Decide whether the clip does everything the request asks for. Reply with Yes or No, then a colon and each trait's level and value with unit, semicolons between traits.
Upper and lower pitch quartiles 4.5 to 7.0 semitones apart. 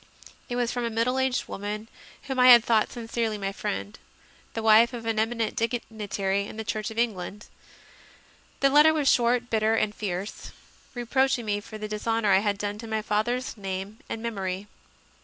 No: narrow, 2.4 semitones